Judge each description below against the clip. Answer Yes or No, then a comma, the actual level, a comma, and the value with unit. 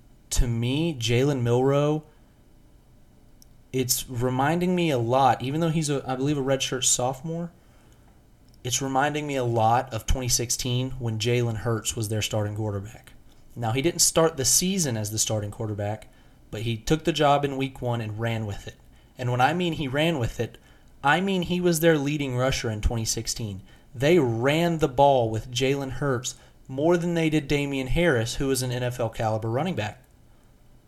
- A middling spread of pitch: Yes, average, 4.1 semitones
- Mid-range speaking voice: No, low, 130 Hz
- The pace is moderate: Yes, average, 175 wpm